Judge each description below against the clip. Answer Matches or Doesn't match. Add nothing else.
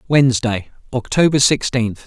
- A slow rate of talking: Matches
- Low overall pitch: Matches